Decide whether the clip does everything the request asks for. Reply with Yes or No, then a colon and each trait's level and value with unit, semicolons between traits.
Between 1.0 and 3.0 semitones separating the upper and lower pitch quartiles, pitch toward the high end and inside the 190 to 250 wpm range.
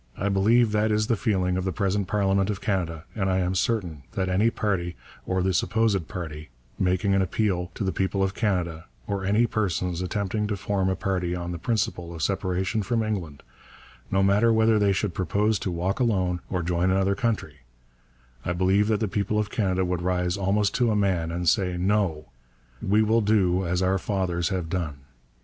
No: narrow, 2.6 semitones; very low, 95 Hz; average, 195 wpm